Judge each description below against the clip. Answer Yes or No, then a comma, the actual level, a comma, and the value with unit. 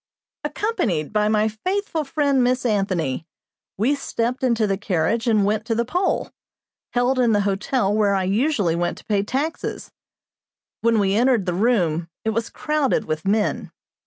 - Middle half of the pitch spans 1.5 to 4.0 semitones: No, average, 4.4 semitones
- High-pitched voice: Yes, high, 220 Hz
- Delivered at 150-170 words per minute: Yes, average, 160 wpm